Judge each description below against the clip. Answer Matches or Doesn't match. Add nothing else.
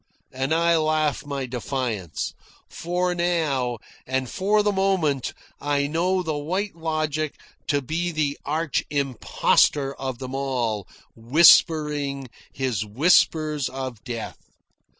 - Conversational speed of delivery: Doesn't match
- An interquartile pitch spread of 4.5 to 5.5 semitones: Doesn't match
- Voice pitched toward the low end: Doesn't match